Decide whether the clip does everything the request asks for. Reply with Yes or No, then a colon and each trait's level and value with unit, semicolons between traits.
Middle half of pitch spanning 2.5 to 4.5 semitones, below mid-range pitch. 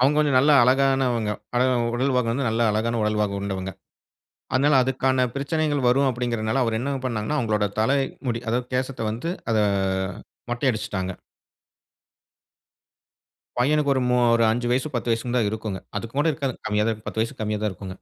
Yes: average, 3.5 semitones; low, 120 Hz